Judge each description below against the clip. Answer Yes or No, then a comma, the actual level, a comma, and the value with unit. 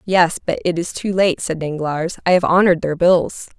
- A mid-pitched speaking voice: Yes, medium, 175 Hz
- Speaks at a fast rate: Yes, fast, 220 wpm